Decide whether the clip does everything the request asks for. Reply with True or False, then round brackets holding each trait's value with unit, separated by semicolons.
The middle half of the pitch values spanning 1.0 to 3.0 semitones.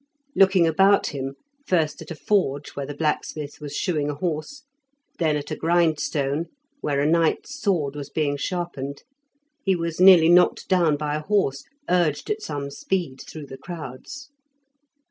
False (3.8 semitones)